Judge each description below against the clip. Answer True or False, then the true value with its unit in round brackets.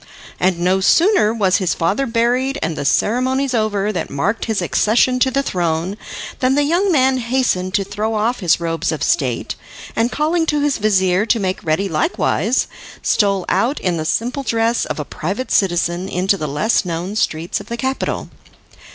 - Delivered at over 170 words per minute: True (180 wpm)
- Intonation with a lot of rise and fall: True (5.9 semitones)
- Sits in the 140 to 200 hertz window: False (210 Hz)